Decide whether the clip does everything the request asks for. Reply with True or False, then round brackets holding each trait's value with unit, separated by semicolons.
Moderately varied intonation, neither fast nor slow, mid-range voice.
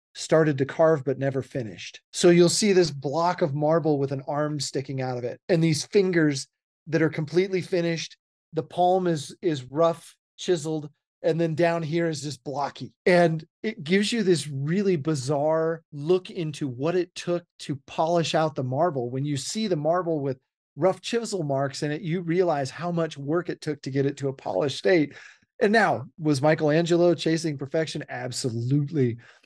True (3.5 semitones; 180 wpm; 160 Hz)